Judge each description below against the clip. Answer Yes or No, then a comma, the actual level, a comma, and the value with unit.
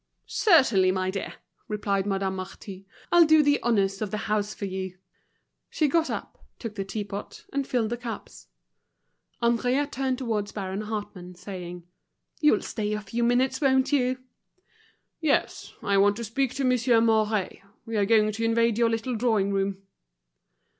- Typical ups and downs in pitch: Yes, average, 4.0 semitones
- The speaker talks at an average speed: Yes, average, 160 wpm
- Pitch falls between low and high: No, high, 220 Hz